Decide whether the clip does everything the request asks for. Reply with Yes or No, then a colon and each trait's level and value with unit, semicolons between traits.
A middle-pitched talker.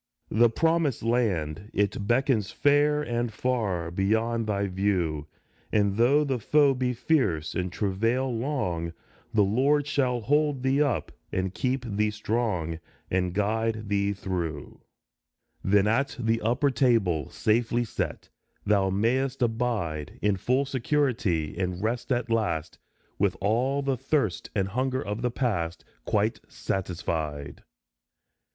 No: low, 110 Hz